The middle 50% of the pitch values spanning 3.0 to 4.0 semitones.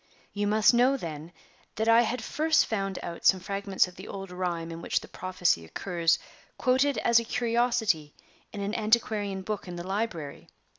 No: average, 4.4 semitones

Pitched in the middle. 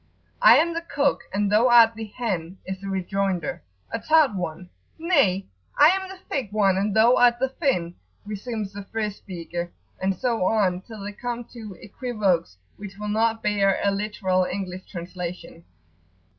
No: high, 205 Hz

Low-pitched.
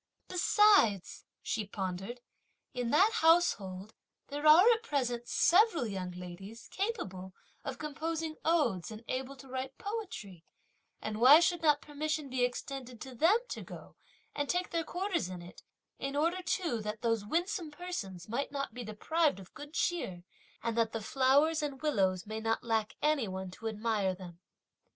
No: very high, 260 Hz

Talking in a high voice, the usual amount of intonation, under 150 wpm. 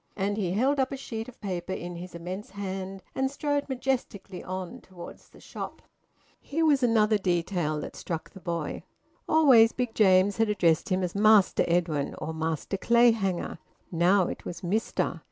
No: high, 195 Hz; average, 4.4 semitones; average, 170 wpm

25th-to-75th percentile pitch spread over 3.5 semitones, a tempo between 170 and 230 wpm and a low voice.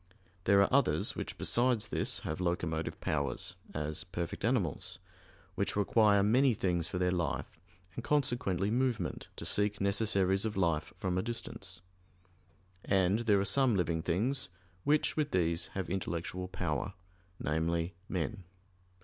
No: average, 4.1 semitones; average, 140 wpm; very low, 95 Hz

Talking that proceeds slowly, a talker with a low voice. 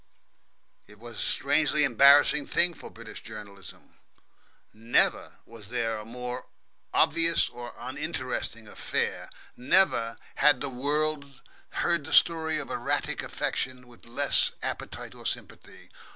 Yes: slow, 125 wpm; low, 130 Hz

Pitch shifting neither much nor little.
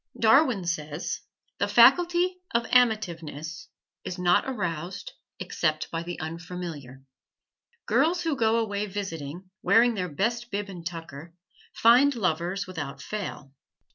No: wide, 5.9 semitones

